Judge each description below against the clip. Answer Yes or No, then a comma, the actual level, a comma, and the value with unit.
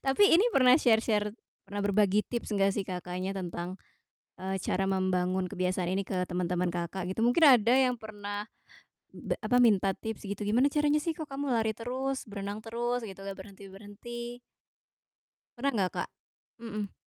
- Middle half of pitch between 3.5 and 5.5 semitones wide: Yes, average, 4.1 semitones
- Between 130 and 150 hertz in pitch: No, high, 205 Hz